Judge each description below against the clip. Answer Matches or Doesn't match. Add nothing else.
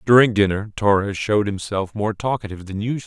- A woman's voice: Doesn't match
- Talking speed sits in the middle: Matches